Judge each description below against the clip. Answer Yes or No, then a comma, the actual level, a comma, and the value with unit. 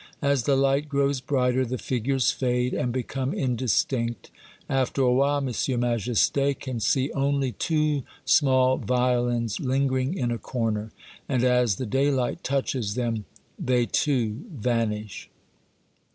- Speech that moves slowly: Yes, slow, 130 wpm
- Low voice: Yes, low, 130 Hz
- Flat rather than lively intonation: Yes, narrow, 2.3 semitones